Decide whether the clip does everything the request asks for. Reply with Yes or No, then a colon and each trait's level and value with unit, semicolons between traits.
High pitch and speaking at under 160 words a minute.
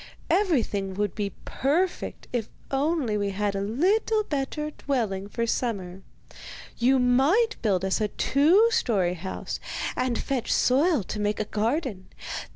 Yes: high, 240 Hz; average, 145 wpm